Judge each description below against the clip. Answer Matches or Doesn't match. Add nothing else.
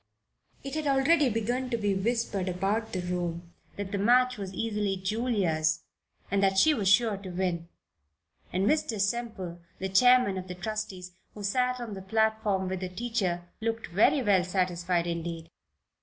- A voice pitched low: Doesn't match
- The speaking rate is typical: Matches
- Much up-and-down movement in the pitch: Doesn't match